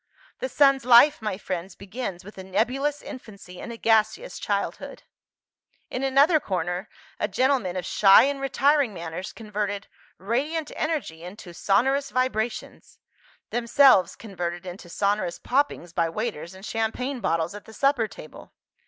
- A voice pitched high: Yes, high, 220 Hz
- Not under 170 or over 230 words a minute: No, average, 140 wpm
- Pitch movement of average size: No, wide, 6.3 semitones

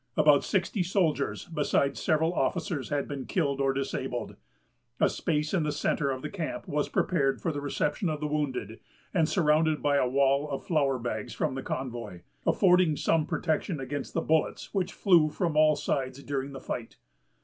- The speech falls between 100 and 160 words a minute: No, average, 180 wpm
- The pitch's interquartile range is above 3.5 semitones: No, average, 2.9 semitones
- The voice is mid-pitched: Yes, medium, 150 Hz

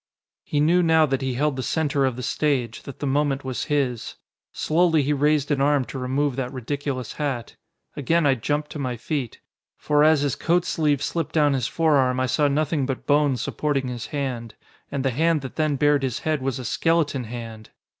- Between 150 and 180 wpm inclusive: No, fast, 205 wpm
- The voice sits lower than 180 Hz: Yes, medium, 140 Hz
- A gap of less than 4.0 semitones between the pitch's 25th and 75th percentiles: Yes, narrow, 2.6 semitones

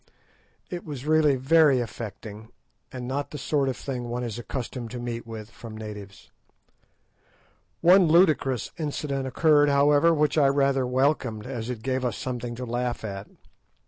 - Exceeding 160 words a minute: No, average, 155 wpm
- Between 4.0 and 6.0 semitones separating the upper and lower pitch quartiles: No, average, 3.6 semitones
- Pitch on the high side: No, low, 130 Hz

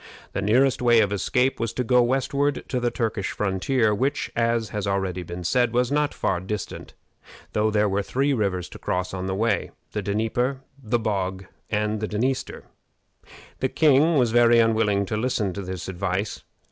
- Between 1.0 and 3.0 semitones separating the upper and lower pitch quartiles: No, average, 4.0 semitones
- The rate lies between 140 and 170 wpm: No, average, 180 wpm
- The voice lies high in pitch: No, low, 110 Hz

